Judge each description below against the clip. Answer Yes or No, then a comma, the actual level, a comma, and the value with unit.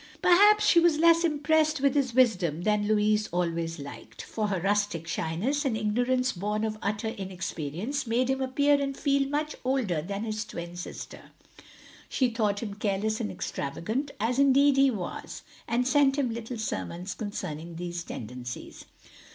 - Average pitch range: No, wide, 7.2 semitones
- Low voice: No, high, 220 Hz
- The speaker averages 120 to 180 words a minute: Yes, average, 160 wpm